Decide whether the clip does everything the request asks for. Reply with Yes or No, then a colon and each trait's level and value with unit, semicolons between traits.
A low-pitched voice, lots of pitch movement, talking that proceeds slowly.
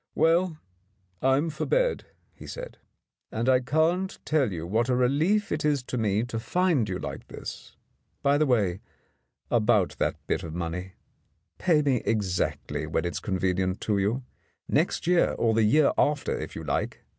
No: low, 125 Hz; wide, 7.2 semitones; average, 170 wpm